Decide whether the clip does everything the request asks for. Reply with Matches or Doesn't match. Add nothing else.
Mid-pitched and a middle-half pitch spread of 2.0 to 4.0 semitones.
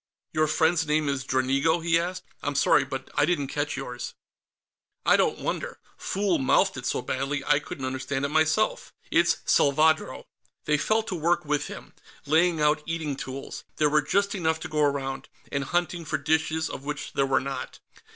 Matches